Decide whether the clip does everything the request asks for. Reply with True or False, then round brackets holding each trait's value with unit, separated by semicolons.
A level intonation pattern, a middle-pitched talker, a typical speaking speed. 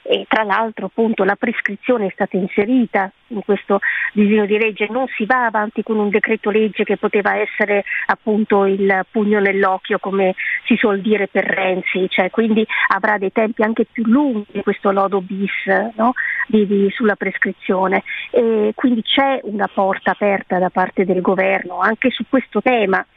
False (2.3 semitones; 210 Hz; 160 wpm)